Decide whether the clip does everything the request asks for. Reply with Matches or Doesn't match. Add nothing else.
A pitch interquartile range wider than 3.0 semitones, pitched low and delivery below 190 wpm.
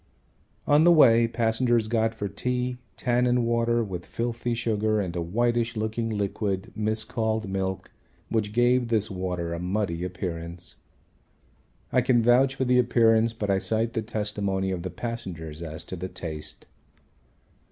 Matches